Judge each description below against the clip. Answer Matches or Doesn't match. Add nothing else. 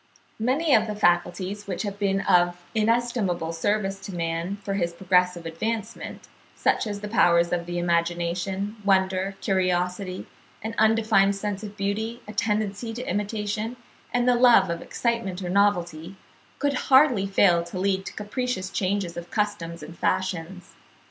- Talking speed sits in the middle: Matches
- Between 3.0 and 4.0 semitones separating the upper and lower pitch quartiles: Matches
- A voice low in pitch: Doesn't match